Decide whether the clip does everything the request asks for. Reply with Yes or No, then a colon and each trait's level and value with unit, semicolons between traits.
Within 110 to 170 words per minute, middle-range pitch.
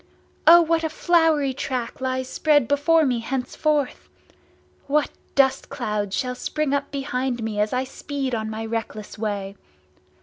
No: average, 145 wpm; very high, 265 Hz